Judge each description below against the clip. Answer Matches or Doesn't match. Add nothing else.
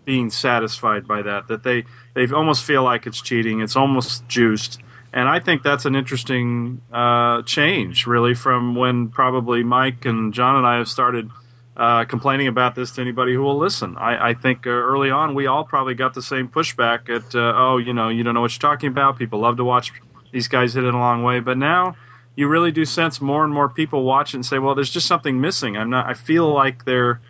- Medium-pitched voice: Doesn't match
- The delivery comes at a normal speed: Doesn't match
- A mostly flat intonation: Matches